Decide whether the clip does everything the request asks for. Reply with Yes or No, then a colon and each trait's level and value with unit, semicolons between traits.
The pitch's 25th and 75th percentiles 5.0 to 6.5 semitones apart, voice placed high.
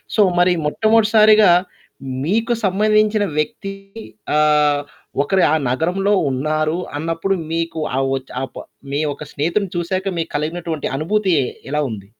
No: average, 5.3 semitones; medium, 175 Hz